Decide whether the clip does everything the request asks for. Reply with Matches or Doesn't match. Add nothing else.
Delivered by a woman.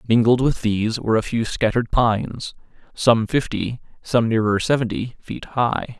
Doesn't match